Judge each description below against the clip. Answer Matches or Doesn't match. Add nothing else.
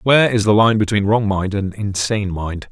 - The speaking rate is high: Matches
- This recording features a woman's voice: Doesn't match